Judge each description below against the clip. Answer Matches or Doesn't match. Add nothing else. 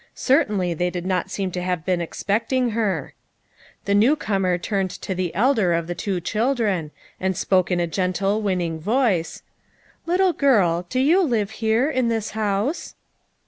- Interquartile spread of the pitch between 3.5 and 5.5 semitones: Matches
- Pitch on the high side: Matches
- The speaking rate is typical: Matches